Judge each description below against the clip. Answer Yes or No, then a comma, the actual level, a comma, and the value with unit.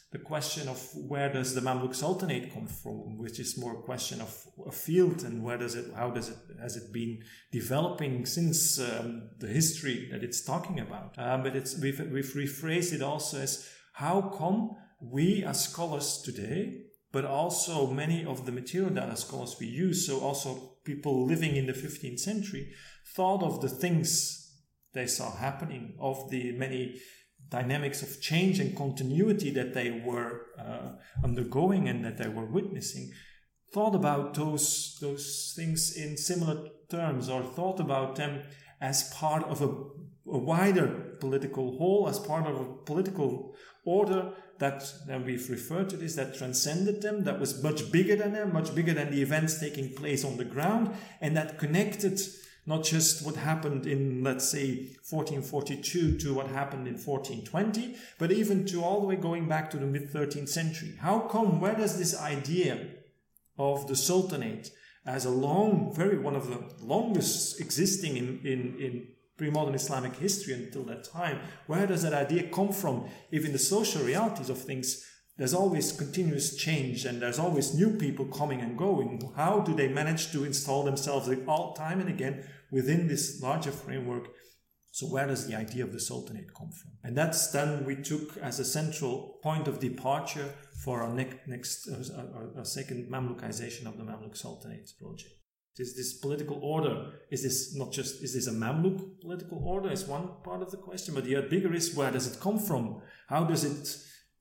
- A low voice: No, medium, 145 Hz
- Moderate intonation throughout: Yes, average, 4.6 semitones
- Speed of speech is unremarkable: Yes, average, 180 wpm